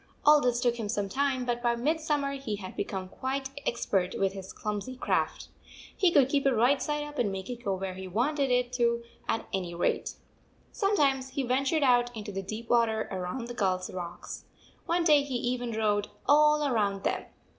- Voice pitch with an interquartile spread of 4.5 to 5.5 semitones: Yes, average, 5.2 semitones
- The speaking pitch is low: No, high, 240 Hz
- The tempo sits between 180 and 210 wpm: Yes, average, 200 wpm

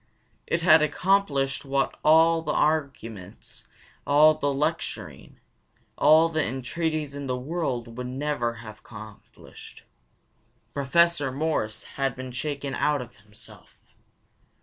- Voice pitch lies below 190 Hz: Yes, medium, 140 Hz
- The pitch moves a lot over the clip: No, average, 3.9 semitones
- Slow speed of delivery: Yes, slow, 115 wpm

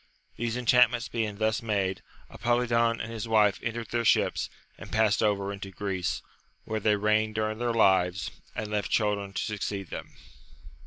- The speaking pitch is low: Yes, low, 110 Hz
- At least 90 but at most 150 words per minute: No, average, 160 wpm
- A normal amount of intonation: No, narrow, 2.3 semitones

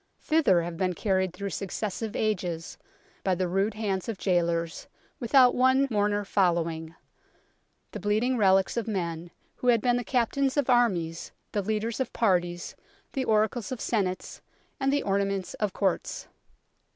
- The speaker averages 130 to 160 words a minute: Yes, average, 150 wpm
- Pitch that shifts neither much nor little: Yes, average, 4.5 semitones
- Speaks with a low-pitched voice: No, high, 200 Hz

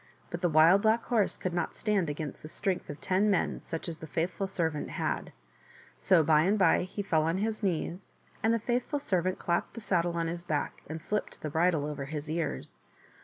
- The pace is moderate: No, fast, 210 wpm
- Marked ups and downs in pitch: No, average, 3.8 semitones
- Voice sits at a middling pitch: Yes, medium, 175 Hz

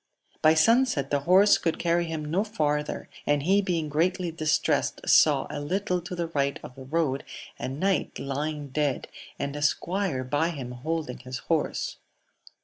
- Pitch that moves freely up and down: No, average, 3.7 semitones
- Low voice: No, medium, 155 Hz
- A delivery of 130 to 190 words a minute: Yes, average, 165 wpm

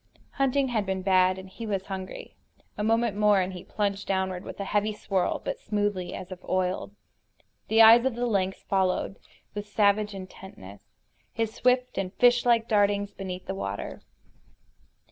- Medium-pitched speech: No, high, 200 Hz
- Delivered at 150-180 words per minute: Yes, average, 165 wpm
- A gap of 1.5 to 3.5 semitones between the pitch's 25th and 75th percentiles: Yes, average, 2.8 semitones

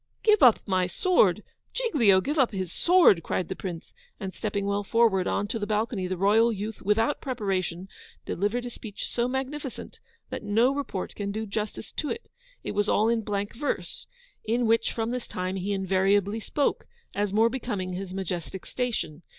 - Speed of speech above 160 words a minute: Yes, average, 180 wpm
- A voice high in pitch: Yes, high, 210 Hz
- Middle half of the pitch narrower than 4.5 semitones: Yes, average, 3.7 semitones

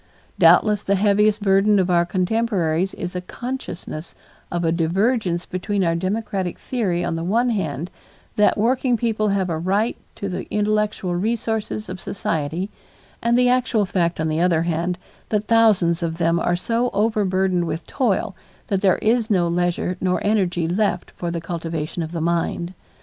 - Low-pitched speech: No, medium, 185 Hz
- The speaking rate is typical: Yes, average, 165 wpm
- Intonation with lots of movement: No, average, 3.7 semitones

